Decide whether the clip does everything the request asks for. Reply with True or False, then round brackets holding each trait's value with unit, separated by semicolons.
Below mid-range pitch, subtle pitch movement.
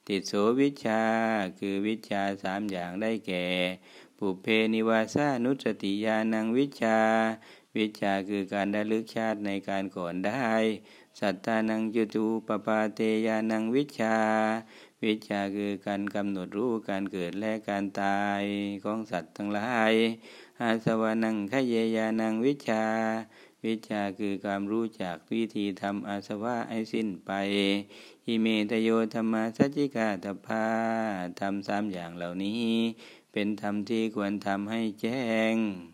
True (110 Hz; 2.0 semitones)